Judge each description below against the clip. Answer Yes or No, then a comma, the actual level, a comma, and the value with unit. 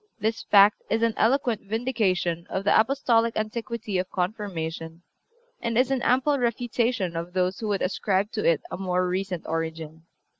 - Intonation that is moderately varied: Yes, average, 4.3 semitones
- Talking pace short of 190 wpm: Yes, average, 160 wpm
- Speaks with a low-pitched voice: No, high, 205 Hz